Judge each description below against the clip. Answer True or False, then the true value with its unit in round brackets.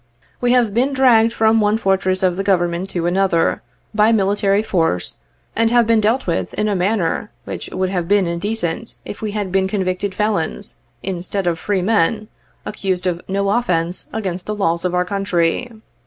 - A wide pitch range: False (3.3 semitones)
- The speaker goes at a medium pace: True (180 wpm)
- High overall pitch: True (195 Hz)